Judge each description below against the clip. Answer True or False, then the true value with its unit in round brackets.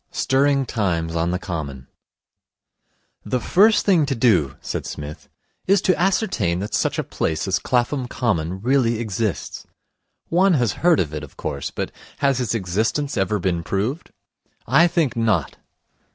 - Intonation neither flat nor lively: False (8.0 semitones)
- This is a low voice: True (115 Hz)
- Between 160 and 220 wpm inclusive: False (150 wpm)